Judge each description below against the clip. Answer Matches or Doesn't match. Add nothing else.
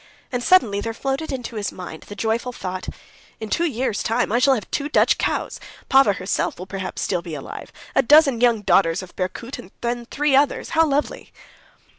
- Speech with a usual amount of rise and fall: Doesn't match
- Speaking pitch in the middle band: Doesn't match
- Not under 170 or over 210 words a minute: Matches